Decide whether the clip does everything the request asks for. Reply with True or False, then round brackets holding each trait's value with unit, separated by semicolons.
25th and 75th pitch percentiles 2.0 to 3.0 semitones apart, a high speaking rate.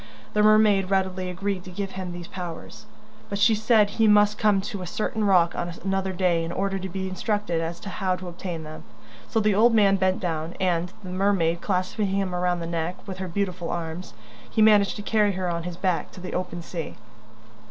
True (2.5 semitones; 215 wpm)